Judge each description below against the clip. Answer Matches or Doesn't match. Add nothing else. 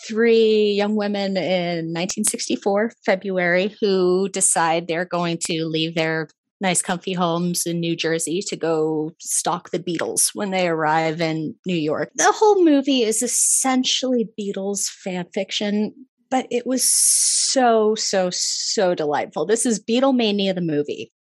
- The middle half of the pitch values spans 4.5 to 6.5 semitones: Matches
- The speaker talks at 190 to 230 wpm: Doesn't match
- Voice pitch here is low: Doesn't match